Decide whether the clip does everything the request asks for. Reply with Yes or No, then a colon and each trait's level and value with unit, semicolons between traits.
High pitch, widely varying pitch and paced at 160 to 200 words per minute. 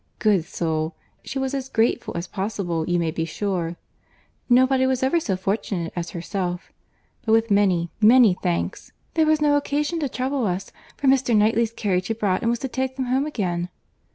Yes: high, 215 Hz; wide, 6.6 semitones; average, 180 wpm